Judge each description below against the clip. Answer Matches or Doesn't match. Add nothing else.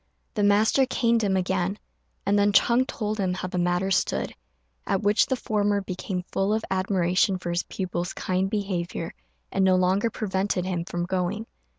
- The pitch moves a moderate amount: Doesn't match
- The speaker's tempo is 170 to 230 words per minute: Matches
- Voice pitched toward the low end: Doesn't match